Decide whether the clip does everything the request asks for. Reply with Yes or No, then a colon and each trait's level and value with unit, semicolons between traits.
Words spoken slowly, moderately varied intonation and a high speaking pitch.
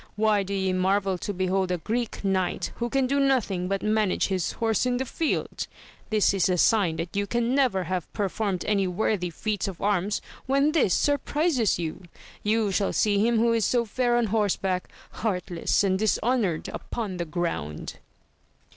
No: average, 175 wpm; average, 3.9 semitones; high, 205 Hz